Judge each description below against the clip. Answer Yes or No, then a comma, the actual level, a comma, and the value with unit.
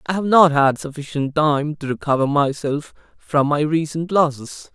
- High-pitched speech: No, medium, 150 Hz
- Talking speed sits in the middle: Yes, average, 165 wpm